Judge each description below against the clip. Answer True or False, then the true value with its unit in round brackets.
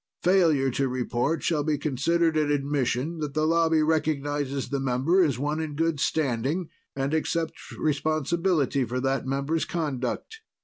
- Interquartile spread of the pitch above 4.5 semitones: False (3.0 semitones)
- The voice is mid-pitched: True (150 Hz)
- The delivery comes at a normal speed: True (145 wpm)